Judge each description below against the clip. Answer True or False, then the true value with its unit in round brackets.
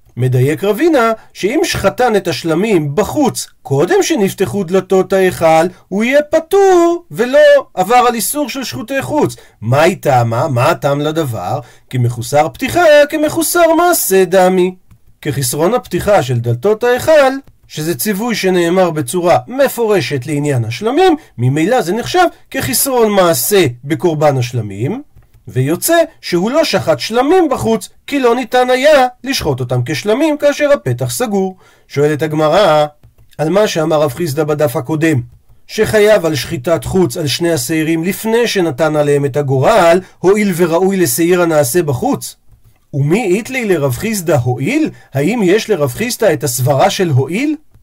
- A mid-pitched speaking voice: True (180 Hz)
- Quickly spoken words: False (135 wpm)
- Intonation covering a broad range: True (8.6 semitones)